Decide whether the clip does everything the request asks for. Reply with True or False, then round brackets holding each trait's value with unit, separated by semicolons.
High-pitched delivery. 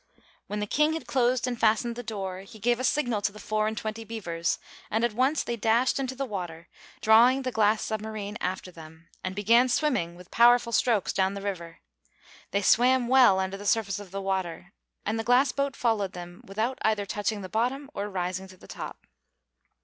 True (215 Hz)